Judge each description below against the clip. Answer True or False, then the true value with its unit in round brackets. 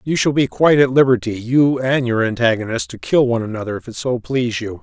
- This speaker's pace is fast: True (210 wpm)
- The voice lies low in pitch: True (125 Hz)